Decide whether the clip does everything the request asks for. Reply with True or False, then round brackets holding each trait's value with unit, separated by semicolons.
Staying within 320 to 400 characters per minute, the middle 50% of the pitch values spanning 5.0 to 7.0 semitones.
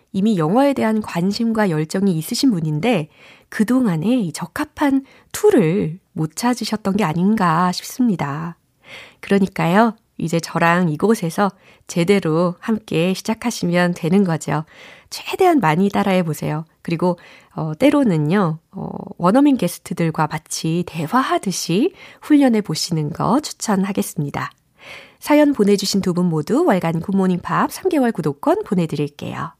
False (290 characters per minute; 5.3 semitones)